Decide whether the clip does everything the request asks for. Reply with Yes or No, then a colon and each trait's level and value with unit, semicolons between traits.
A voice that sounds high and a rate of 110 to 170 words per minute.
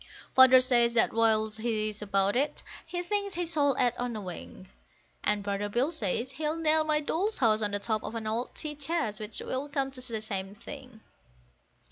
No: high, 240 Hz; average, 200 wpm